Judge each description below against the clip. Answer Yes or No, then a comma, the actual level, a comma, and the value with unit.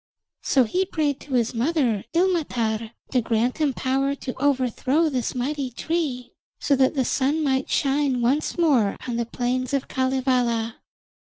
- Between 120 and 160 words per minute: Yes, average, 155 wpm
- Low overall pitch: No, very high, 260 Hz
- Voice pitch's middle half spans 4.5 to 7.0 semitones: No, average, 2.9 semitones